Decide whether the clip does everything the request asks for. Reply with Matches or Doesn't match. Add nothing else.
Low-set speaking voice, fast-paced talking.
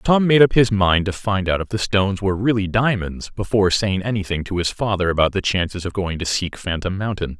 Matches